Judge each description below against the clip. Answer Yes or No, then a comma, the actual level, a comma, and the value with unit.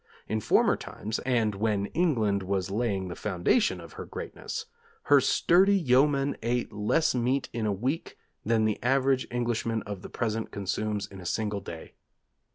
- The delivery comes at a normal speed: Yes, average, 165 wpm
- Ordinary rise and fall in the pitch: Yes, average, 4.2 semitones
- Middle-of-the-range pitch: No, low, 110 Hz